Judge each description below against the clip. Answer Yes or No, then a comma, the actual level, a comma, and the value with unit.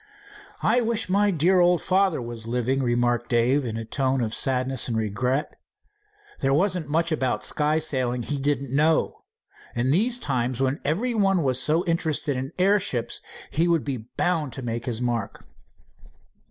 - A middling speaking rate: Yes, average, 160 wpm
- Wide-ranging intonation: Yes, wide, 5.7 semitones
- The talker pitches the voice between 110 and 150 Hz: Yes, low, 135 Hz